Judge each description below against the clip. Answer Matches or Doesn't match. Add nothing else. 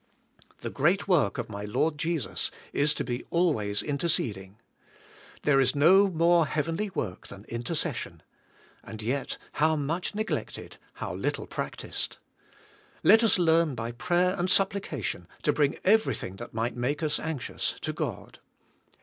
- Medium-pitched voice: Matches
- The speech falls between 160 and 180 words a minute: Doesn't match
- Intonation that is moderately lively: Doesn't match